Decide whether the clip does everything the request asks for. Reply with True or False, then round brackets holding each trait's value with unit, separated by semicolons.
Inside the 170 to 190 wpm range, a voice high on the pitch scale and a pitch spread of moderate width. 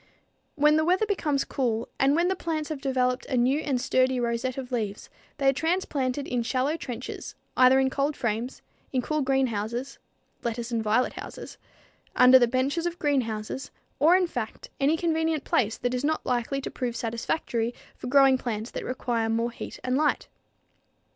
True (175 wpm; 260 Hz; 3.5 semitones)